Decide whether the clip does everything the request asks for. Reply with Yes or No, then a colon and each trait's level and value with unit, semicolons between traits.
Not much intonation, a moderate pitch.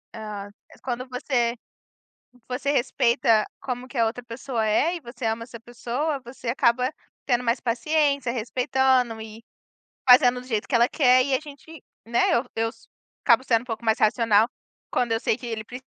No: narrow, 2.2 semitones; high, 245 Hz